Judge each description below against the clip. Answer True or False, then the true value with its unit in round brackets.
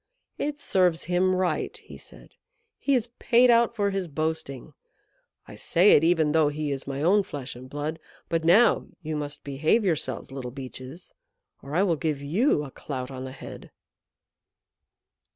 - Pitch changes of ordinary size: True (5.0 semitones)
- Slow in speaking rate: False (165 wpm)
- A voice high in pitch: False (160 Hz)